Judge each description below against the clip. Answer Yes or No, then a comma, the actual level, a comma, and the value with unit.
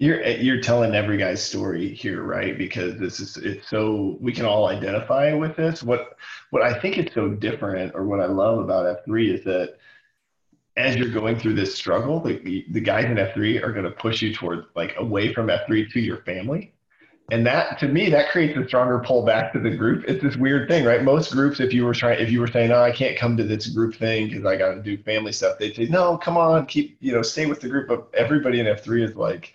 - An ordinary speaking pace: No, fast, 240 wpm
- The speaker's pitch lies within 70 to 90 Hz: No, low, 120 Hz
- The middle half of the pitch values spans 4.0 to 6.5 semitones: Yes, average, 4.3 semitones